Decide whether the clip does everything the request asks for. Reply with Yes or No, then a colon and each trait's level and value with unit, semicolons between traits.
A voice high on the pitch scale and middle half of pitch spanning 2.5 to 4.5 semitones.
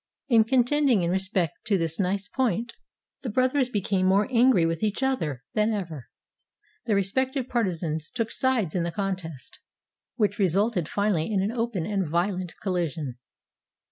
No: high, 200 Hz; average, 5.2 semitones